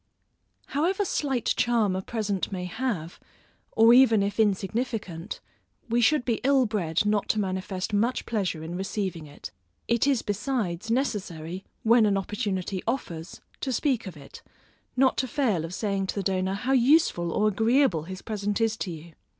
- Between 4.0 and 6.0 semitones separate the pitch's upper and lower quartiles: Yes, average, 4.4 semitones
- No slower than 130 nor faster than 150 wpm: No, average, 165 wpm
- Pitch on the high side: Yes, high, 210 Hz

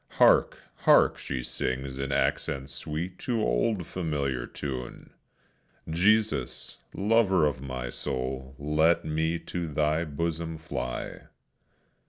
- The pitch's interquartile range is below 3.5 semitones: No, average, 4.2 semitones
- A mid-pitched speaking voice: No, very low, 75 Hz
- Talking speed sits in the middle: No, slow, 115 wpm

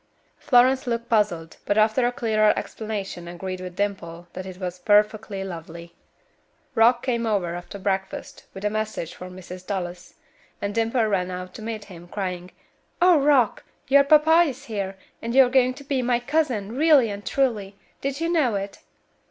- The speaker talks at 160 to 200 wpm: Yes, average, 175 wpm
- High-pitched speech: Yes, high, 210 Hz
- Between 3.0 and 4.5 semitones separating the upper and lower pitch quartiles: No, average, 5.1 semitones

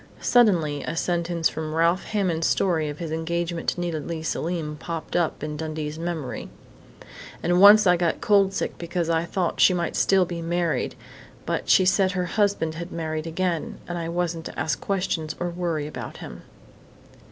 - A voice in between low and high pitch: Yes, medium, 170 Hz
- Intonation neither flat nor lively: No, narrow, 2.0 semitones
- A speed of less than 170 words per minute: No, average, 175 wpm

